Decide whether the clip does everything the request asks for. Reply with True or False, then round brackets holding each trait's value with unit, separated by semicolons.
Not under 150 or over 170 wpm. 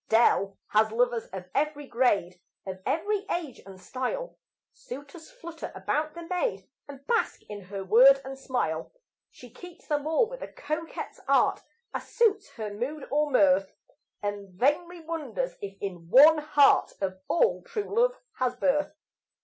True (155 wpm)